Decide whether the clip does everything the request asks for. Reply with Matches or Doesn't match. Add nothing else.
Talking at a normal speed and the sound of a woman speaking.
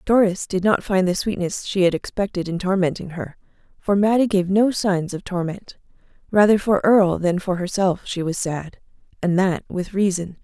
Matches